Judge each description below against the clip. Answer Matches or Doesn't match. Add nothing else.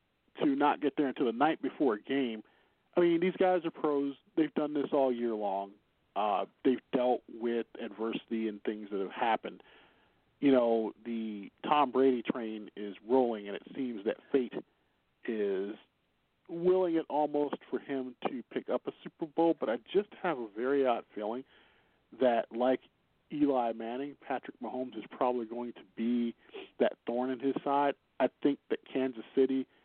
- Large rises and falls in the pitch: Doesn't match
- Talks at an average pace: Matches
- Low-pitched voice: Matches